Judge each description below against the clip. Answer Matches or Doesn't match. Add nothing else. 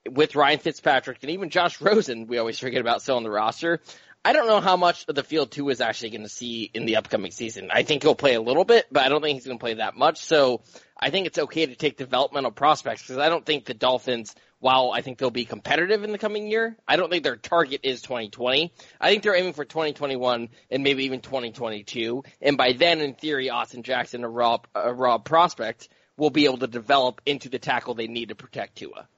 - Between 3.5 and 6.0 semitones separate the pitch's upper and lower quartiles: Matches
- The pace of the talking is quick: Matches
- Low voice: Matches